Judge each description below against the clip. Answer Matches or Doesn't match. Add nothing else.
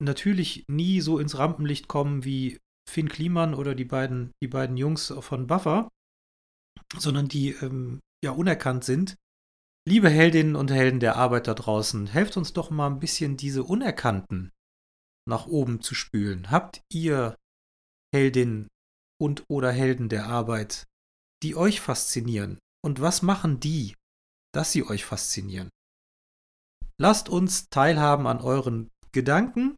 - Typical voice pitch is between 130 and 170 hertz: Matches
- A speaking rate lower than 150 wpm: Matches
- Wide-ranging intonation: Matches